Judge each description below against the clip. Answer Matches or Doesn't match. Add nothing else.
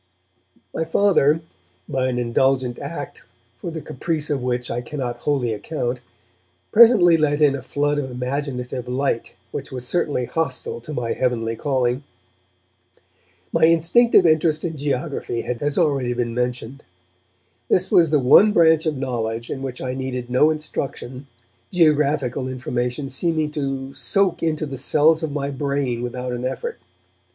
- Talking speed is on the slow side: Doesn't match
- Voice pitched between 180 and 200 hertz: Doesn't match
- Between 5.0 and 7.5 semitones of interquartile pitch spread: Doesn't match